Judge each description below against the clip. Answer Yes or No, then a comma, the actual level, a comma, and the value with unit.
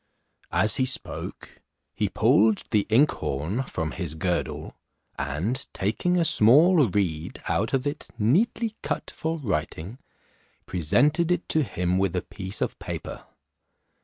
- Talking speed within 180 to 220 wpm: No, slow, 135 wpm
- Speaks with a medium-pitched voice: No, low, 110 Hz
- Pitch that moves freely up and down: Yes, wide, 8.7 semitones